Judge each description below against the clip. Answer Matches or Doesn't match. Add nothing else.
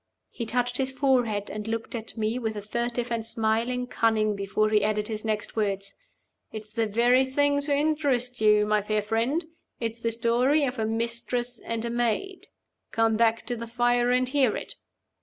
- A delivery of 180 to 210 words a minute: Matches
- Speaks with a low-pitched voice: Doesn't match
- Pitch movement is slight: Matches